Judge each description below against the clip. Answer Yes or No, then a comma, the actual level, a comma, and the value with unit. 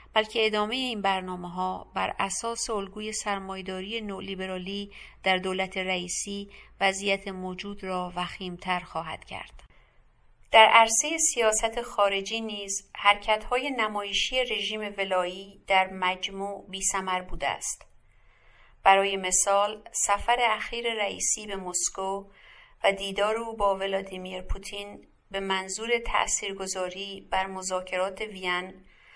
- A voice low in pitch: No, high, 195 Hz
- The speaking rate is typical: No, slow, 110 wpm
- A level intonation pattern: Yes, narrow, 2.3 semitones